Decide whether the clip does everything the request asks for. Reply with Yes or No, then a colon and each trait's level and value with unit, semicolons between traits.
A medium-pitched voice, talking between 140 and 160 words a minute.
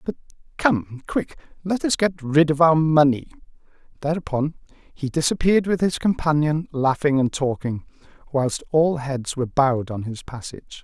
Yes: medium, 150 Hz; average, 150 wpm